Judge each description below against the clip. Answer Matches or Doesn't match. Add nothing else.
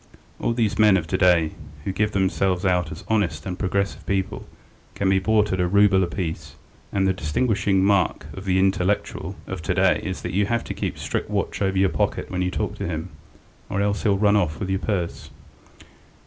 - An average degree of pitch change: Doesn't match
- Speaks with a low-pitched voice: Matches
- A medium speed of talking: Doesn't match